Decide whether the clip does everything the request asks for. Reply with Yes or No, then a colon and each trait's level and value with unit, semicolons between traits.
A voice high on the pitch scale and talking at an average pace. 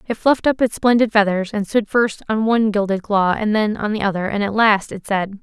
No: high, 210 Hz; fast, 255 wpm